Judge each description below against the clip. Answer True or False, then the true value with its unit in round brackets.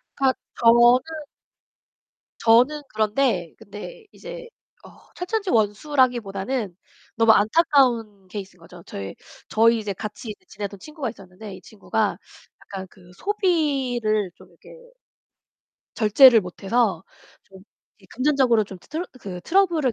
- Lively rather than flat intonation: True (5.7 semitones)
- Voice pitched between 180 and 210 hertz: False (225 Hz)